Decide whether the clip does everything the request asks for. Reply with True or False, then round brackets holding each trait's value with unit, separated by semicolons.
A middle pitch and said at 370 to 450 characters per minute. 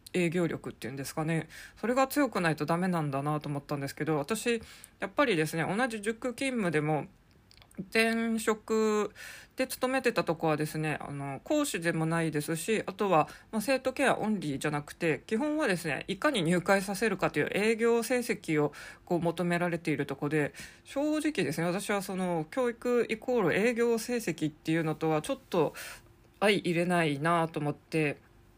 False (175 Hz; 355 characters per minute)